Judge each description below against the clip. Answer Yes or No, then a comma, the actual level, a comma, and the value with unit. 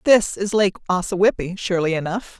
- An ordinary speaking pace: Yes, average, 150 wpm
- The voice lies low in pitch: No, high, 190 Hz